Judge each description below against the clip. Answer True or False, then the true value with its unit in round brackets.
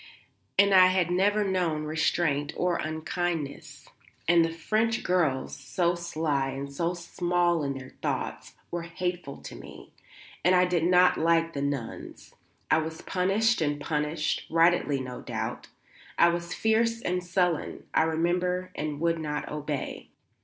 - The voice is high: False (170 Hz)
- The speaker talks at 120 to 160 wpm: True (145 wpm)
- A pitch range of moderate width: True (3.0 semitones)